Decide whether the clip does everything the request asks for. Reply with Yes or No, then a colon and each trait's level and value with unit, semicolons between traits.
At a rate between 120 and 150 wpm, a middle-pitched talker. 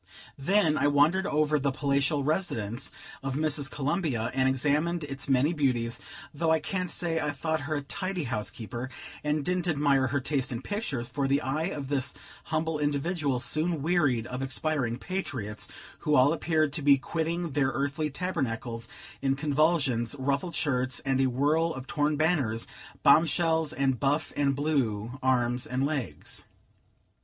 No: average, 160 wpm; medium, 145 Hz